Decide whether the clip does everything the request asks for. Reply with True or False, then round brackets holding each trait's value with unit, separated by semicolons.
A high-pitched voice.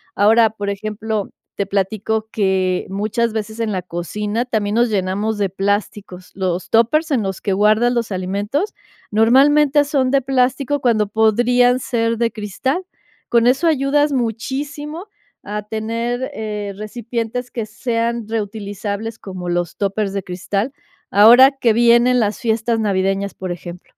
True (220 Hz)